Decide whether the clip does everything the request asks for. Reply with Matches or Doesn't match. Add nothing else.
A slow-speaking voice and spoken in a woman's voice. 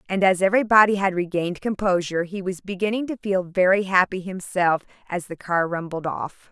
Doesn't match